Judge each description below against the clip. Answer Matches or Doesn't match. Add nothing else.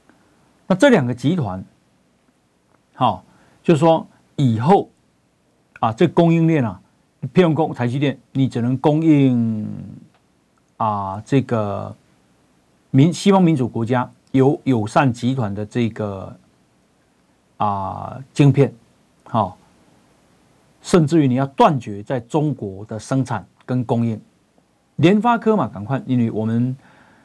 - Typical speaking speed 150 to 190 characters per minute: Matches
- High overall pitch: Doesn't match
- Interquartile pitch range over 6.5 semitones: Doesn't match